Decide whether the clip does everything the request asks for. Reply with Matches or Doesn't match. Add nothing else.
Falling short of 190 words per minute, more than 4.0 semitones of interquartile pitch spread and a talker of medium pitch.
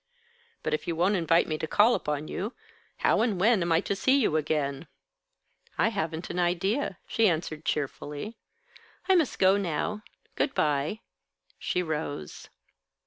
Matches